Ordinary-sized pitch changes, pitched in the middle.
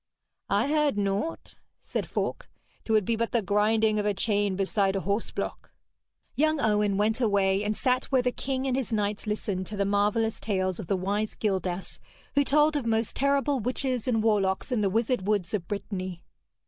No: average, 3.7 semitones; high, 210 Hz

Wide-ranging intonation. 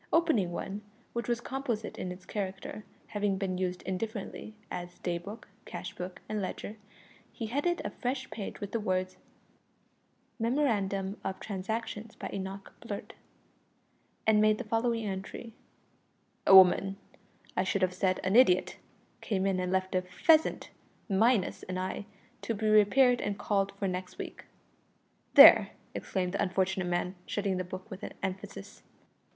No: average, 2.9 semitones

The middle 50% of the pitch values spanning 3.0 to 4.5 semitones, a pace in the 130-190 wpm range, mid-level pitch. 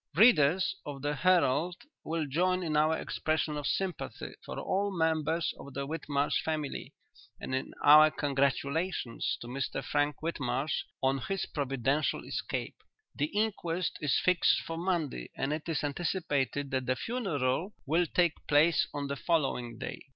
Yes: average, 3.6 semitones; average, 150 wpm; medium, 150 Hz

